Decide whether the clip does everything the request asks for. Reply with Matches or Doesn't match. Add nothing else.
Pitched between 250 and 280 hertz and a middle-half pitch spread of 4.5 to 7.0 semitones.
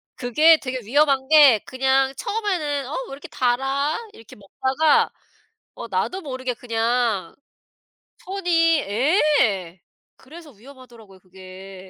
Matches